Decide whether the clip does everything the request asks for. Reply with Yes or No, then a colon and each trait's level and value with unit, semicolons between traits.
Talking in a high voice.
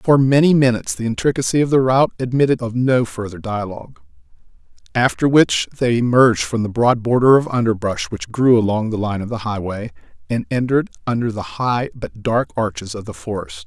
No: low, 115 Hz